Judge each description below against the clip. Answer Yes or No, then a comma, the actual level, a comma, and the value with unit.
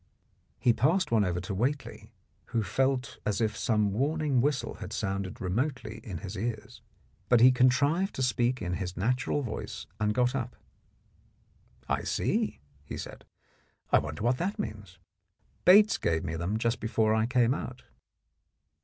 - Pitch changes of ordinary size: Yes, average, 4.1 semitones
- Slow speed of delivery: No, average, 155 wpm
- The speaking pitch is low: Yes, low, 115 Hz